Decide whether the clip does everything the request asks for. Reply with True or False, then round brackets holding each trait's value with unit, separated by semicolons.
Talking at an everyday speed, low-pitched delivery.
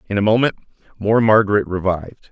True (155 wpm; 105 Hz)